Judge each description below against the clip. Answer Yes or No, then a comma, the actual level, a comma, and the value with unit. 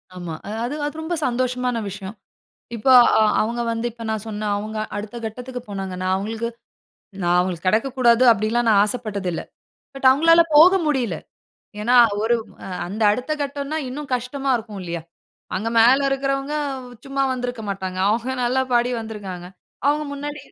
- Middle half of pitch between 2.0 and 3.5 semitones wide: No, average, 4.5 semitones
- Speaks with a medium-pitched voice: No, high, 235 Hz